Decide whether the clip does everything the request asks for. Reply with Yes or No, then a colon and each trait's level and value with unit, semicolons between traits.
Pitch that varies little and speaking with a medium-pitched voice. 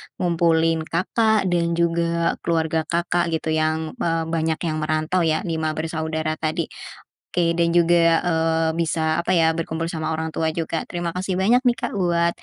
Yes: narrow, 1.2 semitones; medium, 165 Hz